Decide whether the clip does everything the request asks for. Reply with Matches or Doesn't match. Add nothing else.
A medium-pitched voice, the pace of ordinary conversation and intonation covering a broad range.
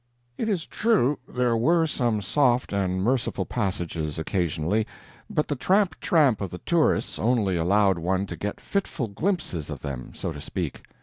Doesn't match